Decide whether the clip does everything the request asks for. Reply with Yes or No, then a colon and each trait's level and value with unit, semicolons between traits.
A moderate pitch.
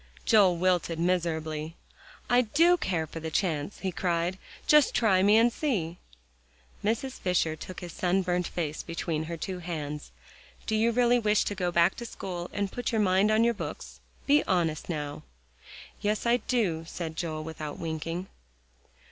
Yes: medium, 180 Hz